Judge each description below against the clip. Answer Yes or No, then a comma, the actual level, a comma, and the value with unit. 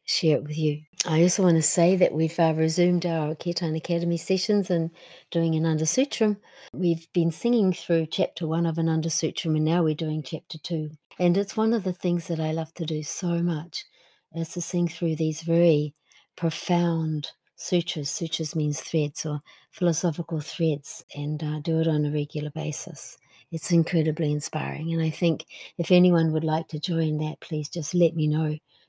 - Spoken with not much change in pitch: Yes, narrow, 1.7 semitones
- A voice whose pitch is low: No, medium, 165 Hz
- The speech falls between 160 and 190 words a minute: Yes, average, 185 wpm